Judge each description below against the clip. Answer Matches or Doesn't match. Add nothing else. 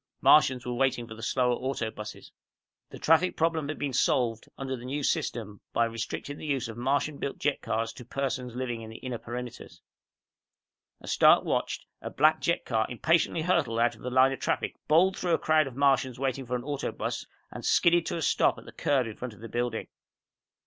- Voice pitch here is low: Matches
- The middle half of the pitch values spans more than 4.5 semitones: Doesn't match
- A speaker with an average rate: Doesn't match